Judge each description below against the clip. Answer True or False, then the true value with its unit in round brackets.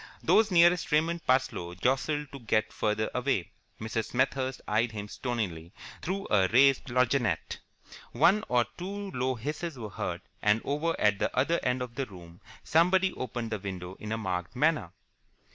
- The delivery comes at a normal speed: True (160 wpm)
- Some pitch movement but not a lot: False (6.1 semitones)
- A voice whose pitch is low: True (125 Hz)